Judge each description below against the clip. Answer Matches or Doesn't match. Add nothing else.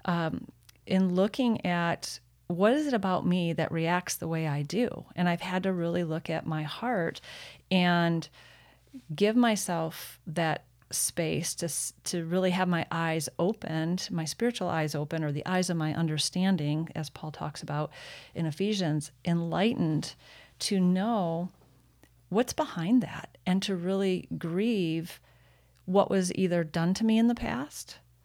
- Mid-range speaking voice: Matches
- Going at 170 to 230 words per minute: Doesn't match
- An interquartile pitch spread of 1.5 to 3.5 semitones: Matches